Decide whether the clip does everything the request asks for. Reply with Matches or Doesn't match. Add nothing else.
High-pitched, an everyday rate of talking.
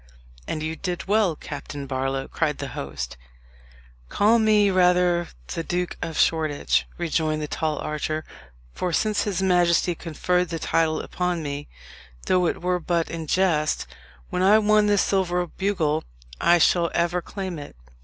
Doesn't match